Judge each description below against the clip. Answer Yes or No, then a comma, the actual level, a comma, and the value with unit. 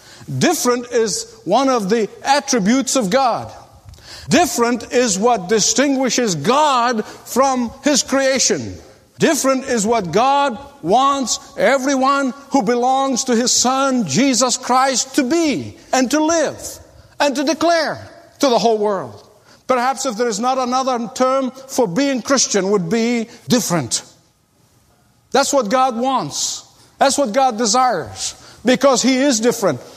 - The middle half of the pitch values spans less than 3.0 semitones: Yes, narrow, 2.6 semitones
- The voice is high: Yes, very high, 255 Hz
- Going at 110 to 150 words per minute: Yes, slow, 135 wpm